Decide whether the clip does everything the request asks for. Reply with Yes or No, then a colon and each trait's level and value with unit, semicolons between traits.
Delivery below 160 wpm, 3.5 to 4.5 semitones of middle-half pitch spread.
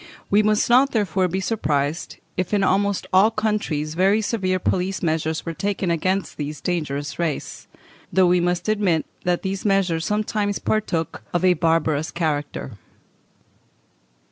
Yes: average, 140 wpm; average, 3.8 semitones